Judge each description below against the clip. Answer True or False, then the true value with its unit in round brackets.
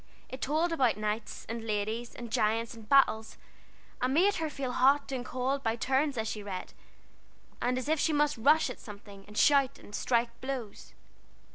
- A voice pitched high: True (250 Hz)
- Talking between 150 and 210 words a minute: True (180 wpm)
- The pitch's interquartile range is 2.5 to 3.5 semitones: False (4.0 semitones)